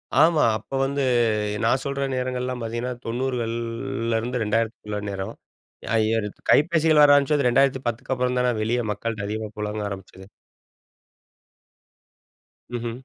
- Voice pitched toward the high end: No, low, 120 Hz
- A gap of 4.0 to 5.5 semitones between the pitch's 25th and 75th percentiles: No, average, 3.3 semitones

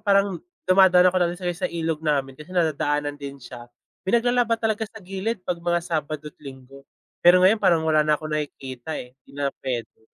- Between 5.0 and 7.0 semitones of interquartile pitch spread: No, average, 4.5 semitones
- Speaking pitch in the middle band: Yes, medium, 165 Hz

